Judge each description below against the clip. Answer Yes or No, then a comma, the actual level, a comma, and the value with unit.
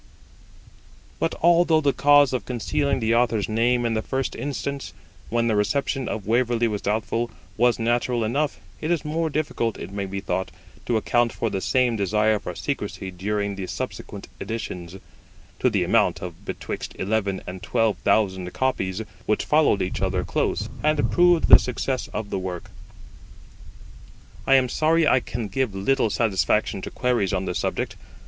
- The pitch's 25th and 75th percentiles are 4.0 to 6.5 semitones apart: Yes, average, 4.8 semitones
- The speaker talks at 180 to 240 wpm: No, average, 165 wpm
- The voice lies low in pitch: Yes, low, 115 Hz